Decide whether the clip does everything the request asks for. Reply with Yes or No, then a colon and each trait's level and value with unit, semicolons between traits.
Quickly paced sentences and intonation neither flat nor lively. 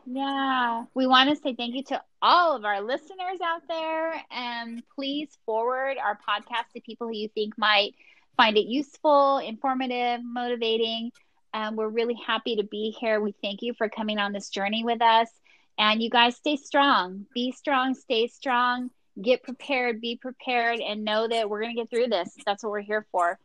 No: average, 190 wpm; average, 3.4 semitones